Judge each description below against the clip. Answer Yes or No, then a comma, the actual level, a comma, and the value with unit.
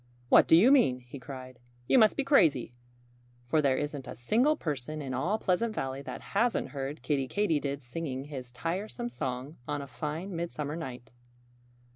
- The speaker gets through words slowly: No, average, 170 wpm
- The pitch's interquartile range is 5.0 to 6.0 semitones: Yes, wide, 5.4 semitones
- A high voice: No, medium, 145 Hz